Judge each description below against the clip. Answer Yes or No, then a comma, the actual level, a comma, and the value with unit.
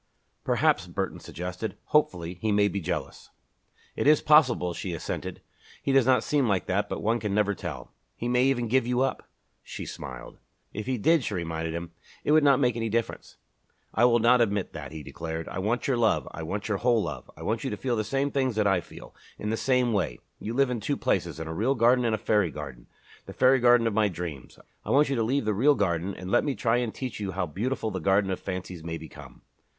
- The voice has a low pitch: Yes, low, 110 Hz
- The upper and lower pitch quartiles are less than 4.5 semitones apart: No, average, 5.3 semitones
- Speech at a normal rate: No, fast, 235 wpm